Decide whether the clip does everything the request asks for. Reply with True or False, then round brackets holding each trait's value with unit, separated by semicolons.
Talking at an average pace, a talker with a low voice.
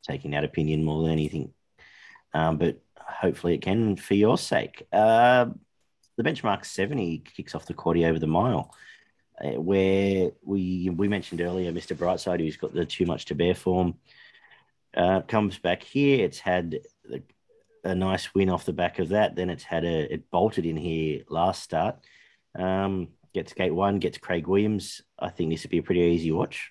True (185 wpm; 90 Hz)